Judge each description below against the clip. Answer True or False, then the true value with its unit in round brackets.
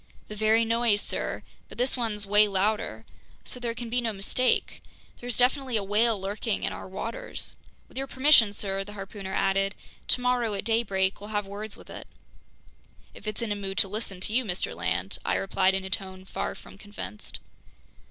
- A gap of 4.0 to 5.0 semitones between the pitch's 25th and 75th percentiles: False (3.0 semitones)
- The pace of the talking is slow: False (190 wpm)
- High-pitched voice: True (210 Hz)